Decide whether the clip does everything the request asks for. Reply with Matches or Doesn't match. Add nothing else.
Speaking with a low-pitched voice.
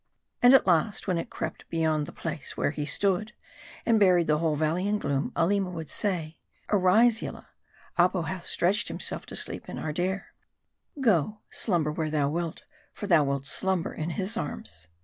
Doesn't match